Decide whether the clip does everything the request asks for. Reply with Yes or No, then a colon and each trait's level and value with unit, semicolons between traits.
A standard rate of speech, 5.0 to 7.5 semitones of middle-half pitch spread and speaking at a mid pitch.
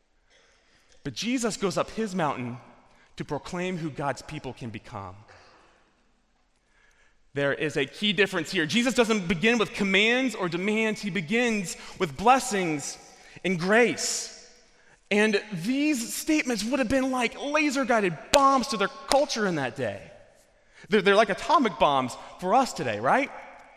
No: average, 145 wpm; wide, 5.5 semitones; high, 210 Hz